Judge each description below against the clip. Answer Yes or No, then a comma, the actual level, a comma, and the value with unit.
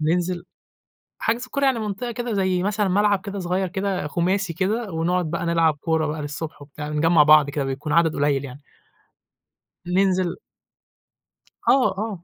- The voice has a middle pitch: Yes, medium, 180 Hz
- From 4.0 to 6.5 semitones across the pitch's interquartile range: Yes, average, 4.5 semitones